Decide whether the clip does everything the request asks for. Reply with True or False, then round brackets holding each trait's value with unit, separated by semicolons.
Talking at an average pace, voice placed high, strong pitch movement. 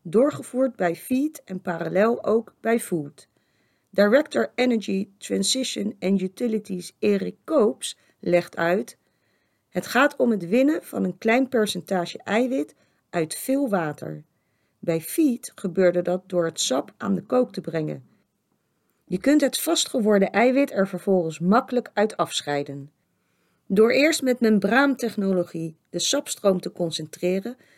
False (130 wpm; 200 Hz; 5.7 semitones)